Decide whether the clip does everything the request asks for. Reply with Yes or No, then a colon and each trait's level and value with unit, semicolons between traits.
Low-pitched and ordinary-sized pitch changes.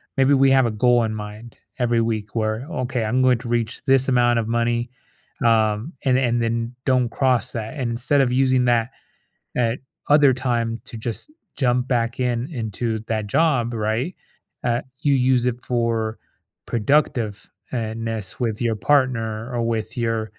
No: low, 120 Hz; narrow, 2.1 semitones